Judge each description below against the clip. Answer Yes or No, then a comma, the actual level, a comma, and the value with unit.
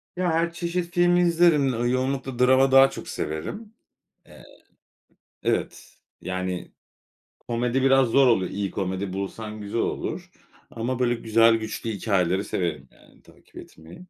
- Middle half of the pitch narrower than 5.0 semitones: No, average, 5.3 semitones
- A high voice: No, low, 120 Hz